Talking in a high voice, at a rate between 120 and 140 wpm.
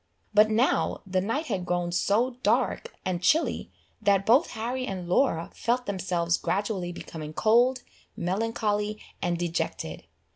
Yes: high, 205 Hz; slow, 135 wpm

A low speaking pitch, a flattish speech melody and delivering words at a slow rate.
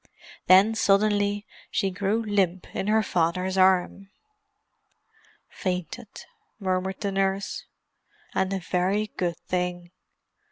No: high, 190 Hz; narrow, 1.8 semitones; slow, 105 wpm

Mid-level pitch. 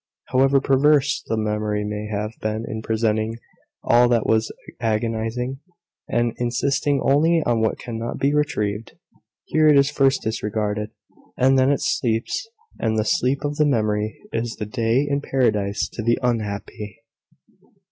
No: low, 115 Hz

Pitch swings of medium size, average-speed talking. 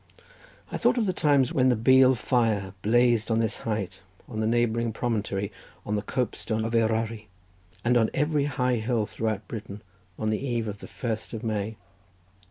No: narrow, 2.3 semitones; average, 180 wpm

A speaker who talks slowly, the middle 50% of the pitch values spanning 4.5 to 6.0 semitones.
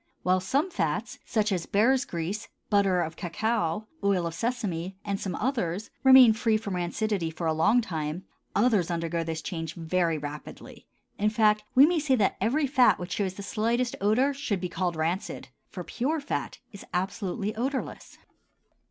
No: average, 170 wpm; average, 5.3 semitones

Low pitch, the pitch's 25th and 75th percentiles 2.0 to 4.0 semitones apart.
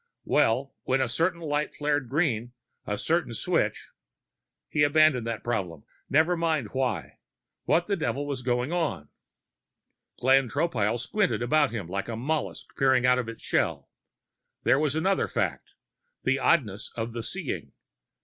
No: low, 130 Hz; average, 4.8 semitones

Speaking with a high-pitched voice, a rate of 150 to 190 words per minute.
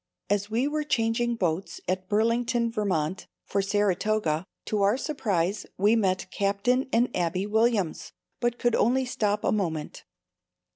No: high, 210 Hz; average, 140 wpm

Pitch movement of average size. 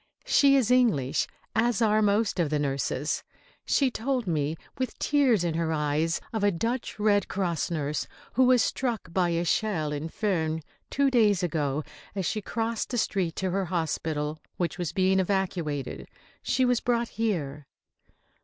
No: wide, 6.1 semitones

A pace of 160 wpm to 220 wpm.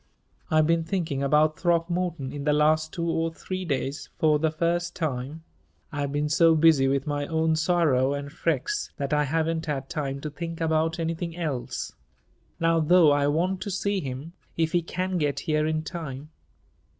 Yes: average, 180 wpm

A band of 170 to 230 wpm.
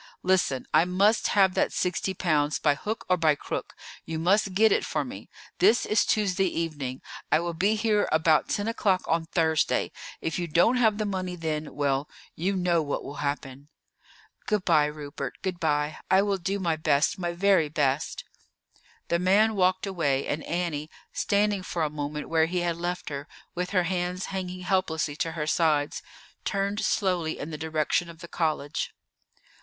Yes: average, 180 wpm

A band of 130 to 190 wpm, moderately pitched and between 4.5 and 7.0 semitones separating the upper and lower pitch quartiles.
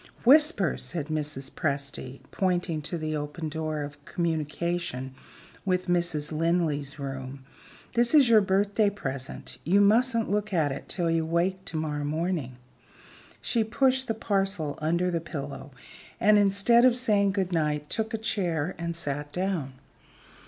Yes: average, 145 wpm; medium, 170 Hz; average, 5.2 semitones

